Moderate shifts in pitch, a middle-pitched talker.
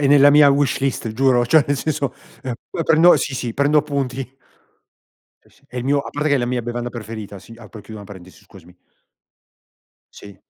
No: average, 3.9 semitones; low, 130 Hz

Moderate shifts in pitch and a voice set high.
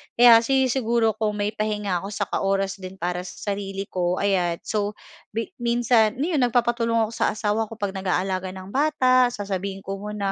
Yes: average, 3.2 semitones; high, 210 Hz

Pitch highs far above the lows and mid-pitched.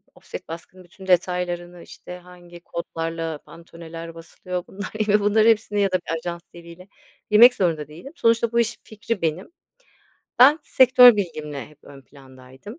No: average, 4.1 semitones; medium, 180 Hz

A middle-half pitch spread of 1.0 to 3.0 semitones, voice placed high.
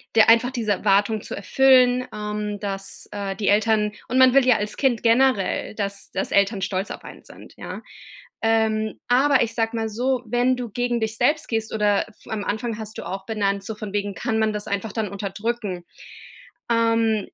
Yes: average, 2.7 semitones; high, 220 Hz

